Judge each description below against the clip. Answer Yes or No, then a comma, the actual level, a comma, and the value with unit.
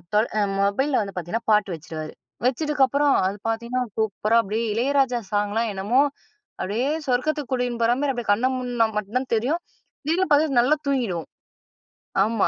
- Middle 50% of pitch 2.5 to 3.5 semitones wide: No, average, 4.3 semitones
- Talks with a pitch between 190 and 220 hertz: No, high, 235 Hz